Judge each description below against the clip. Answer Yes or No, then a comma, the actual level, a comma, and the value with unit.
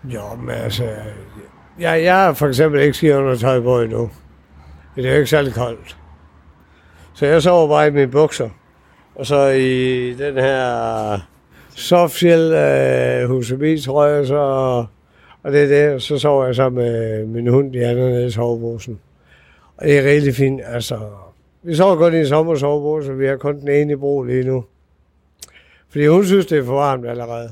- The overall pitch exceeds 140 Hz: No, low, 130 Hz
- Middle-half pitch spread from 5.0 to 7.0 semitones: Yes, average, 5.3 semitones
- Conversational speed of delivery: Yes, average, 175 wpm